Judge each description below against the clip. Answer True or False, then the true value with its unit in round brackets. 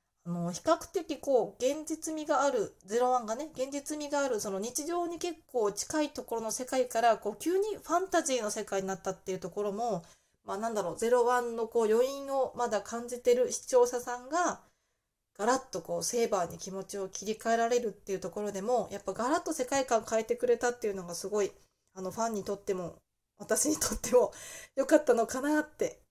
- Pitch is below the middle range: False (240 Hz)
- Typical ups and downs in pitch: False (5.8 semitones)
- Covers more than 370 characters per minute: True (400 characters per minute)